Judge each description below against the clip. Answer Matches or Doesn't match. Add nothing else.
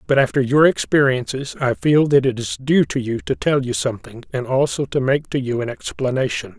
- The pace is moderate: Doesn't match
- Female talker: Doesn't match